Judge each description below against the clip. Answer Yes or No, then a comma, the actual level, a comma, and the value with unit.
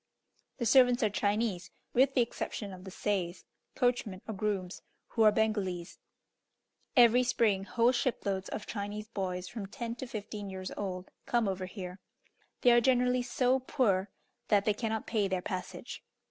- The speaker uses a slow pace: No, average, 160 wpm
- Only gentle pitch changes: No, average, 3.9 semitones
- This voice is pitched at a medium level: No, high, 210 Hz